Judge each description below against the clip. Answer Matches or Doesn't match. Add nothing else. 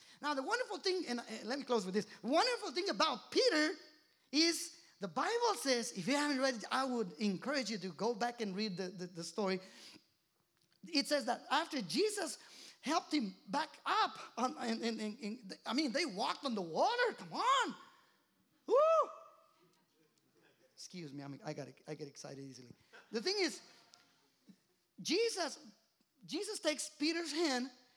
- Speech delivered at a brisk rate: Doesn't match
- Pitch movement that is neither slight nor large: Doesn't match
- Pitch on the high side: Matches